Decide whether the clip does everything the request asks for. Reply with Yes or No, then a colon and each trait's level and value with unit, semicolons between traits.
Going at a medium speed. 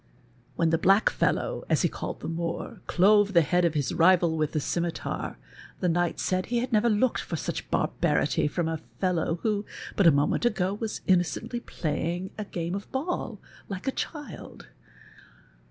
Yes: average, 180 wpm